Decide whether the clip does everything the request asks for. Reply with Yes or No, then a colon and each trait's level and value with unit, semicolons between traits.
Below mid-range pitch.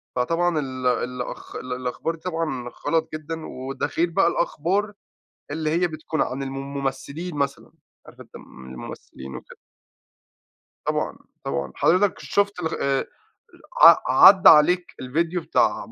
No: medium, 155 Hz